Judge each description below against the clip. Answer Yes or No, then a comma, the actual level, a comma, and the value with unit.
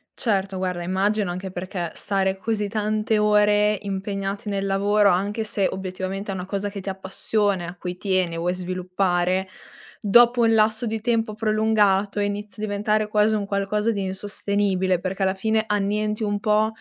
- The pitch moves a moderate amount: No, narrow, 1.9 semitones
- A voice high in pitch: Yes, high, 200 Hz